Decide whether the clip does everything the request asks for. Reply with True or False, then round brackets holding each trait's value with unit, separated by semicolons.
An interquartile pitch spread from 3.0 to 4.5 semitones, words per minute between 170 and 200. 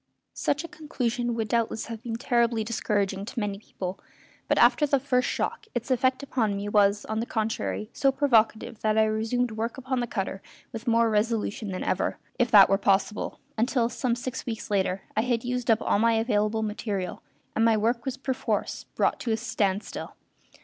False (2.5 semitones; 190 wpm)